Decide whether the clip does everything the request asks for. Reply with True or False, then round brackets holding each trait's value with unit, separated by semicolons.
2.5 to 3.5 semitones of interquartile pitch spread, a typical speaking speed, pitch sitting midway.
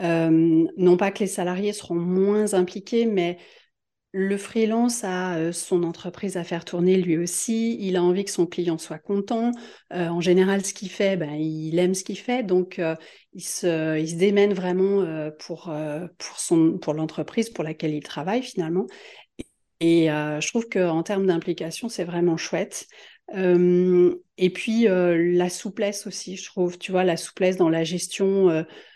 True (2.8 semitones; 185 wpm; 180 Hz)